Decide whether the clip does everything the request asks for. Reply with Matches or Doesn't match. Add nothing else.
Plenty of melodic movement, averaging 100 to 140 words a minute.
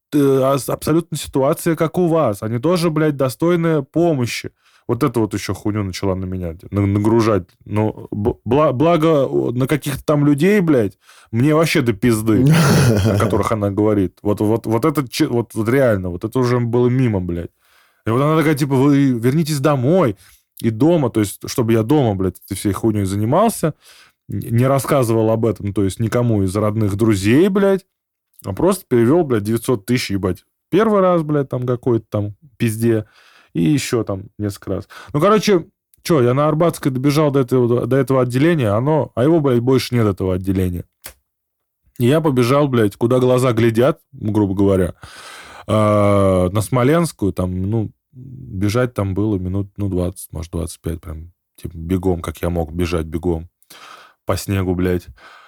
Doesn't match